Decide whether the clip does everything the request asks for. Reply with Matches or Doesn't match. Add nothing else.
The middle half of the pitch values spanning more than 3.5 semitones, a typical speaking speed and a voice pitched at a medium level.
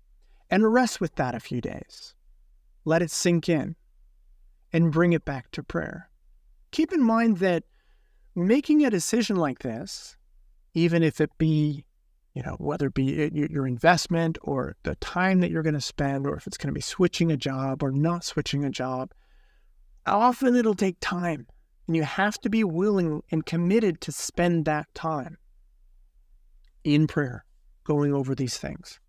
Matches